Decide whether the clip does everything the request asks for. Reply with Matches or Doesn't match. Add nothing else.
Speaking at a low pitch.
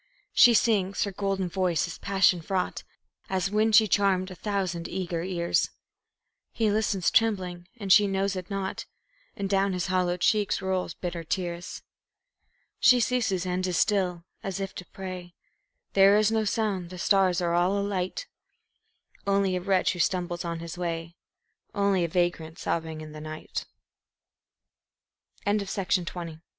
Doesn't match